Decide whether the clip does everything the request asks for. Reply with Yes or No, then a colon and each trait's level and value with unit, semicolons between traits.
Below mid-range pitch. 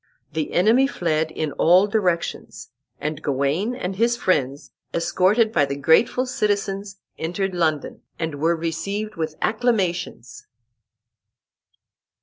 No: medium, 180 Hz